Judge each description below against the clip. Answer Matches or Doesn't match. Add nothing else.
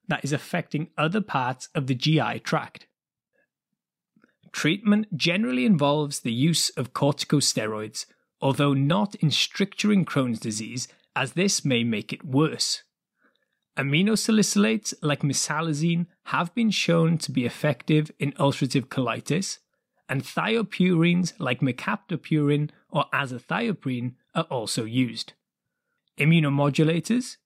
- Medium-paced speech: Doesn't match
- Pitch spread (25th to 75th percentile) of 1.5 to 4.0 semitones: Doesn't match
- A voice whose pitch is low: Doesn't match